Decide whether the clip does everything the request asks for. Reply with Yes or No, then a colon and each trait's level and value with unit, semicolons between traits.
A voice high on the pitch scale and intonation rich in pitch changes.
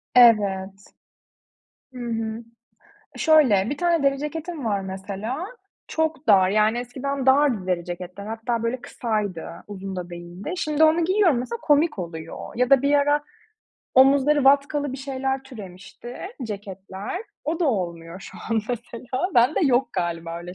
Yes: high, 240 Hz; wide, 6.5 semitones